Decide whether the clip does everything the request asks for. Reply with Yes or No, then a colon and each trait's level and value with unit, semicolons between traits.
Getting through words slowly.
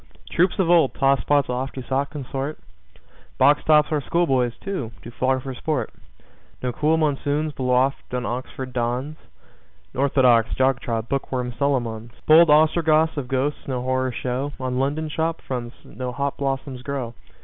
No: average, 160 wpm